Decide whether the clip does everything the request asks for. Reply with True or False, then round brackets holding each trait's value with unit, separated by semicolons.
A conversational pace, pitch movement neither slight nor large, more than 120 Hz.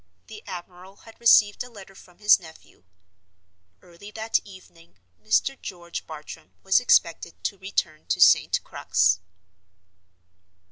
False (125 wpm; 3.7 semitones; 190 Hz)